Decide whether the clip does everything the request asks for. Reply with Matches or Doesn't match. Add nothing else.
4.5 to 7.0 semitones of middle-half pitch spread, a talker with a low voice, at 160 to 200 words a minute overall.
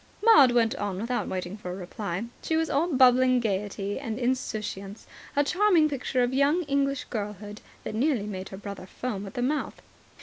Doesn't match